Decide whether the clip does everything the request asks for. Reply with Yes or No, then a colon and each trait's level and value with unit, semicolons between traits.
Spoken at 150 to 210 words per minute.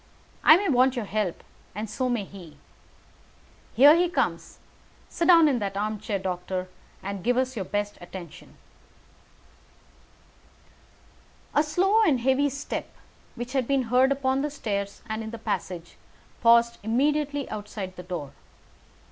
No: average, 140 wpm